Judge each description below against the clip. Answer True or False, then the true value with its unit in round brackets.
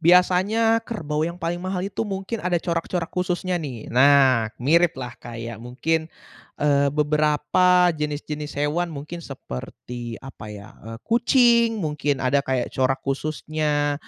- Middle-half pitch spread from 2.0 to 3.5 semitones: False (4.7 semitones)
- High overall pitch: False (150 Hz)